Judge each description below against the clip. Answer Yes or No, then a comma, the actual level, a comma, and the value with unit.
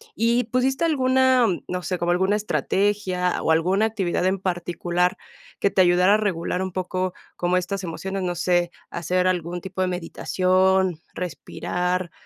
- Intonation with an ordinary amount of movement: No, narrow, 2.0 semitones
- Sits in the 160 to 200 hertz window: Yes, medium, 185 Hz